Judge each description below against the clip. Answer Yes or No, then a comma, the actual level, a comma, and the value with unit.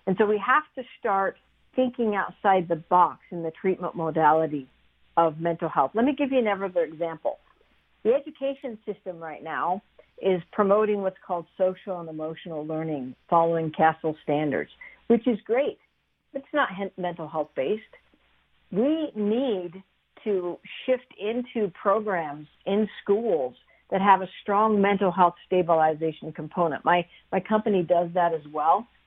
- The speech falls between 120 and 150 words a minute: Yes, average, 140 wpm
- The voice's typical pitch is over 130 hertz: Yes, high, 190 Hz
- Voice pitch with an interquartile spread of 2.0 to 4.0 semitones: No, average, 4.7 semitones